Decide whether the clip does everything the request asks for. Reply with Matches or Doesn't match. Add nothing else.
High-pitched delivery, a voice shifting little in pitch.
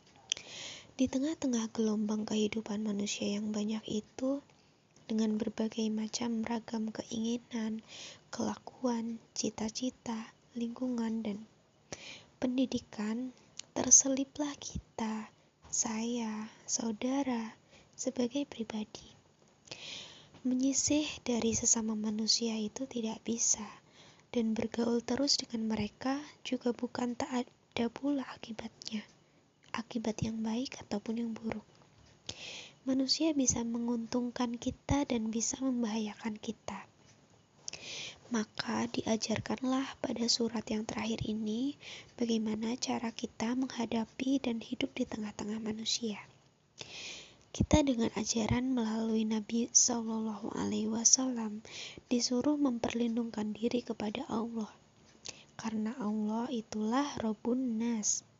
Matches